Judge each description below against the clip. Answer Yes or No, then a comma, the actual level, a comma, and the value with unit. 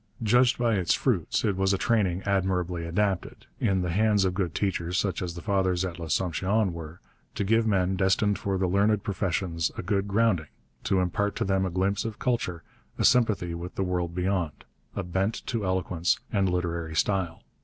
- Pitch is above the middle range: No, very low, 95 Hz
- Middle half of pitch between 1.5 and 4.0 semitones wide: Yes, narrow, 2.5 semitones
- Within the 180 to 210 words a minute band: Yes, average, 185 wpm